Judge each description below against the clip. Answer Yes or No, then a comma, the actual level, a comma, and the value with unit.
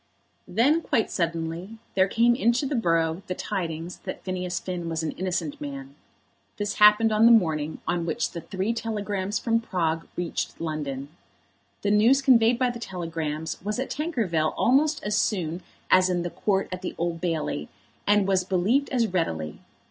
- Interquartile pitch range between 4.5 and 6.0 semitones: Yes, average, 5.3 semitones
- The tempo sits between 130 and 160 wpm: No, average, 170 wpm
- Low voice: No, medium, 185 Hz